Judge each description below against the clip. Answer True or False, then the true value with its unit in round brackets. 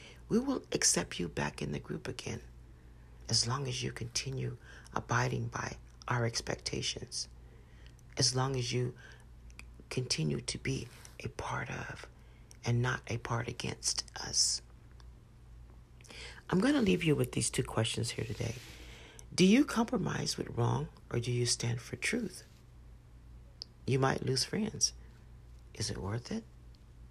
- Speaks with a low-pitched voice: True (115 Hz)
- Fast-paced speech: False (140 wpm)